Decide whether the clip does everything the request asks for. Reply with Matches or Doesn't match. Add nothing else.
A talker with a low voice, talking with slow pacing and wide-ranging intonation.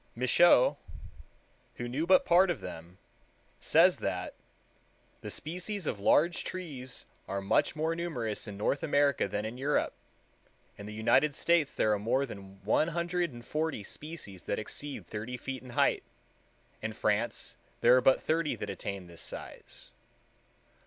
Doesn't match